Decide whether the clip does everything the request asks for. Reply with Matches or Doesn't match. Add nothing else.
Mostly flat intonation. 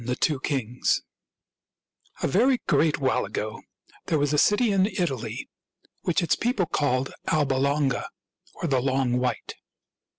Doesn't match